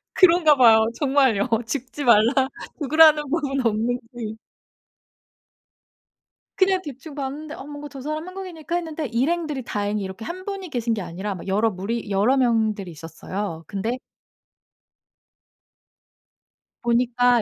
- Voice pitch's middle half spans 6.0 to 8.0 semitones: No, wide, 5.6 semitones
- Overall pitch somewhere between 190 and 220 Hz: No, very high, 250 Hz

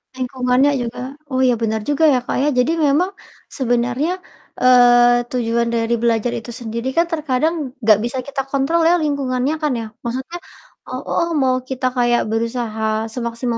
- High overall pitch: Yes, very high, 250 Hz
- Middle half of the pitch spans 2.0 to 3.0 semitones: Yes, narrow, 2.4 semitones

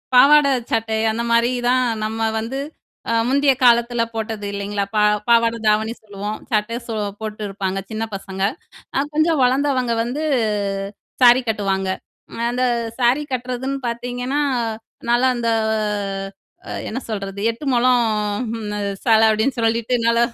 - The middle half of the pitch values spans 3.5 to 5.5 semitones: No, average, 2.7 semitones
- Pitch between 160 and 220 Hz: No, high, 230 Hz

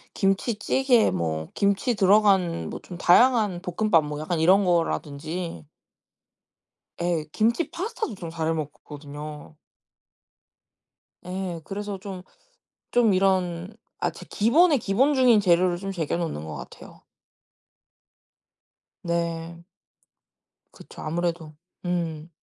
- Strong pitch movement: No, average, 3.8 semitones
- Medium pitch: Yes, medium, 180 Hz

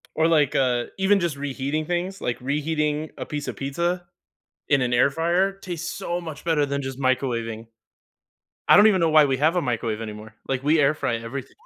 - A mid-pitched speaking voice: Yes, medium, 145 Hz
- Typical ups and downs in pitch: Yes, average, 4.3 semitones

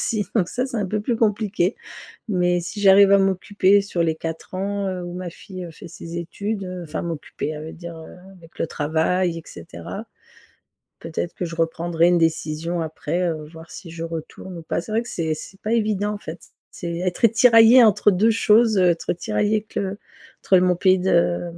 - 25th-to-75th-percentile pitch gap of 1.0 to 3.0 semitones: No, average, 3.5 semitones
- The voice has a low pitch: No, medium, 180 Hz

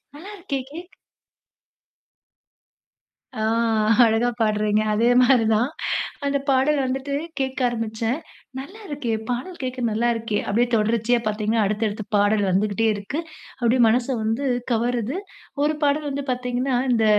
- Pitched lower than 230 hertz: No, high, 240 Hz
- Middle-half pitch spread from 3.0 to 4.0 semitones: Yes, average, 3.7 semitones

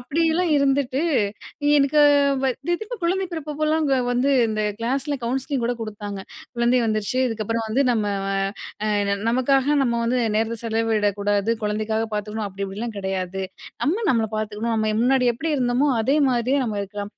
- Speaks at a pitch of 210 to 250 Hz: Yes, high, 240 Hz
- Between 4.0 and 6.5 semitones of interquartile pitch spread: Yes, average, 4.4 semitones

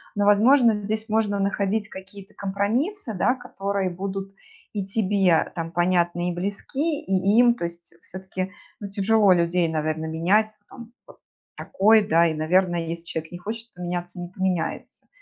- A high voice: Yes, high, 195 Hz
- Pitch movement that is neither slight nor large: Yes, average, 3.4 semitones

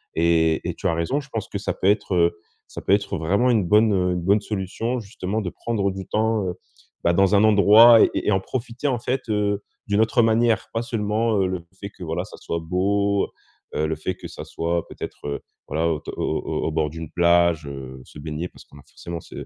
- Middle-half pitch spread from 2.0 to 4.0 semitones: No, average, 4.4 semitones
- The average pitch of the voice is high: No, very low, 95 Hz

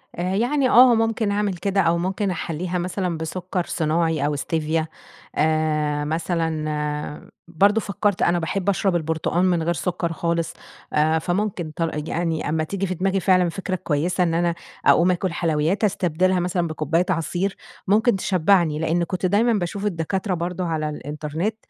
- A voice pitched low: No, medium, 175 Hz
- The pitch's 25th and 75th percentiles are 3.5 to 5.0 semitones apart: No, average, 3.0 semitones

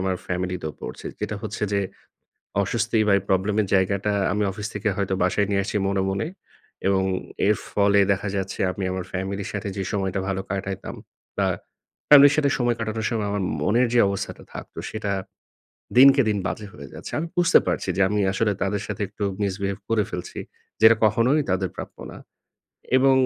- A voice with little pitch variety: Yes, narrow, 2.3 semitones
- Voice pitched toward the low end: Yes, low, 100 Hz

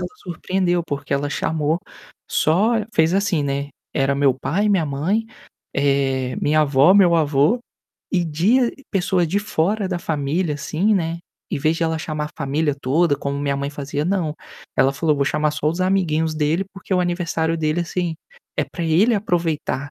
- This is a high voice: No, medium, 160 Hz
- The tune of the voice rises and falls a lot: No, average, 3.8 semitones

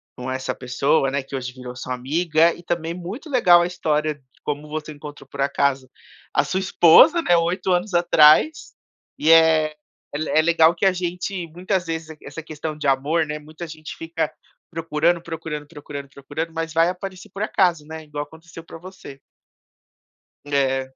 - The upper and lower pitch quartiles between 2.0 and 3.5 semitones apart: Yes, average, 2.8 semitones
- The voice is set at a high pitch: No, medium, 160 Hz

